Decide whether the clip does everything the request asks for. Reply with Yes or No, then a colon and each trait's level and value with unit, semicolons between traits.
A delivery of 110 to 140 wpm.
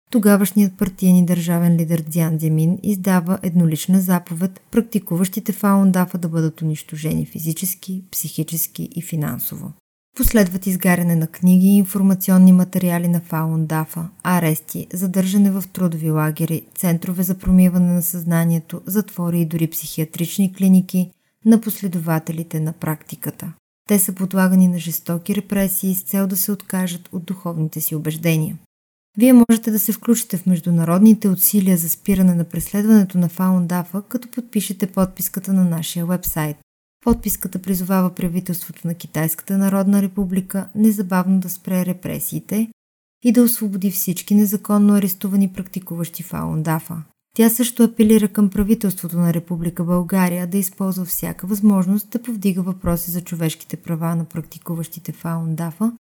Yes: average, 130 wpm